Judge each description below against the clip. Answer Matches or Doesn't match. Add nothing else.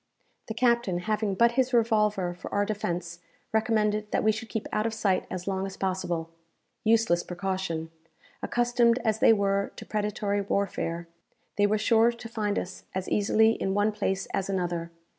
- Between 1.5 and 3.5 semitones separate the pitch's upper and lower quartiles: Matches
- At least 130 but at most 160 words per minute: Doesn't match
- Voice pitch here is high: Matches